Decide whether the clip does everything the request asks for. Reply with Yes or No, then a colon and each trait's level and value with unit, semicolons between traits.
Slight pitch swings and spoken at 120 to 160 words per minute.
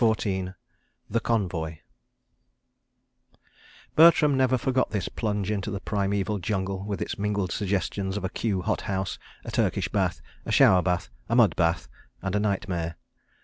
Yes: narrow, 2.3 semitones; average, 150 wpm